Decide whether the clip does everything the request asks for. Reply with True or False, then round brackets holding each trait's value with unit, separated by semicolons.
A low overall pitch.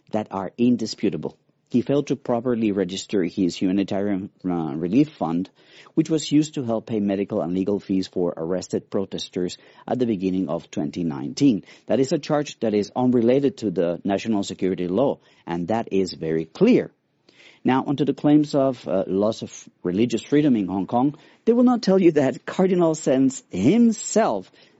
True (110 Hz)